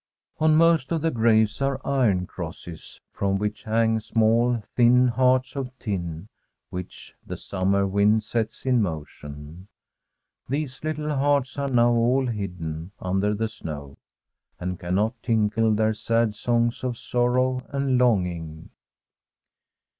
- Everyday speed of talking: No, slow, 130 wpm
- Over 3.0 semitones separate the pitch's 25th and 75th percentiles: Yes, average, 4.8 semitones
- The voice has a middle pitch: No, low, 110 Hz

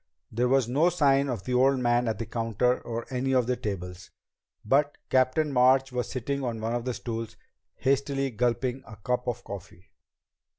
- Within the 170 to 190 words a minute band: Yes, average, 180 wpm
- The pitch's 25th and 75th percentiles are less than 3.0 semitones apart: Yes, narrow, 2.6 semitones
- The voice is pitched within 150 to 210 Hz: No, low, 125 Hz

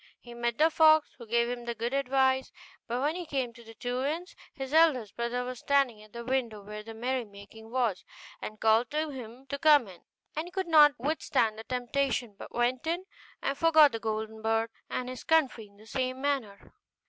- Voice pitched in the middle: No, very high, 250 Hz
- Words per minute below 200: No, fast, 205 wpm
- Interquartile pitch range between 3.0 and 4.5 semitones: Yes, average, 3.8 semitones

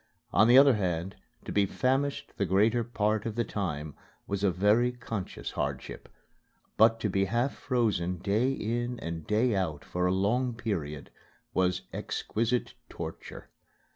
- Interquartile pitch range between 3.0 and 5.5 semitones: Yes, average, 4.4 semitones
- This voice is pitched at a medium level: No, low, 105 Hz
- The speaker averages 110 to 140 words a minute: No, average, 150 wpm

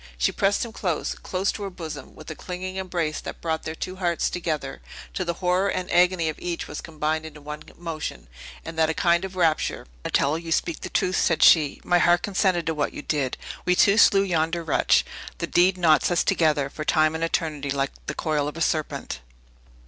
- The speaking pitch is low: No, medium, 165 Hz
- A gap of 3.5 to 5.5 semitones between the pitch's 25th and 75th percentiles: No, narrow, 2.6 semitones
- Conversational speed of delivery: No, fast, 215 wpm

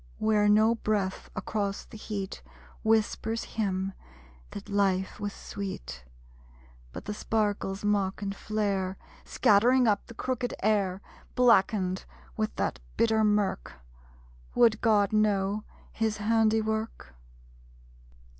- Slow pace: Yes, slow, 110 wpm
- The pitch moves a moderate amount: No, narrow, 1.8 semitones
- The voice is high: Yes, high, 210 Hz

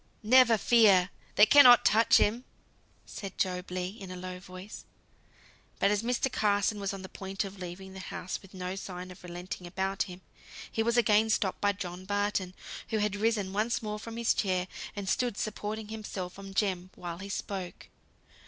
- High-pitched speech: Yes, high, 200 Hz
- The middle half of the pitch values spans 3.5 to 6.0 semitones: No, average, 2.7 semitones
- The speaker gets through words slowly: No, average, 180 wpm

